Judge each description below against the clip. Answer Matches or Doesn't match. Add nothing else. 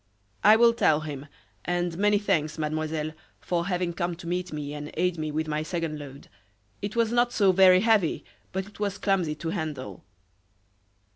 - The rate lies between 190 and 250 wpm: Doesn't match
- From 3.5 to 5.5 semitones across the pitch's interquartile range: Matches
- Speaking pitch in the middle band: Matches